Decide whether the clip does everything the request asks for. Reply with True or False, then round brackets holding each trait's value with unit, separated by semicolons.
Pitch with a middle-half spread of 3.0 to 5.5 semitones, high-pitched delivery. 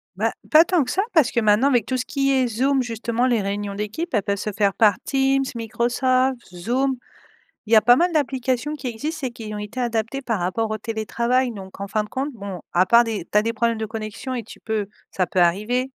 True (3.7 semitones; 235 Hz)